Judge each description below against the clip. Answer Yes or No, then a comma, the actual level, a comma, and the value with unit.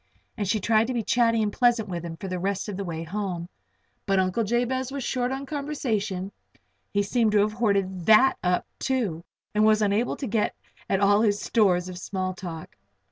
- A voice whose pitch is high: Yes, high, 210 Hz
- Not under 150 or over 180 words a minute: No, average, 195 wpm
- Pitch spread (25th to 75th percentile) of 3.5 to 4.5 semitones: Yes, average, 3.8 semitones